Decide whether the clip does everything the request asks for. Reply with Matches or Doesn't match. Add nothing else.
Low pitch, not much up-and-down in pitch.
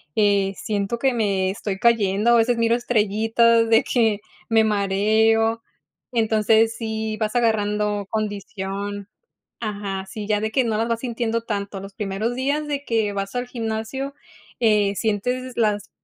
Doesn't match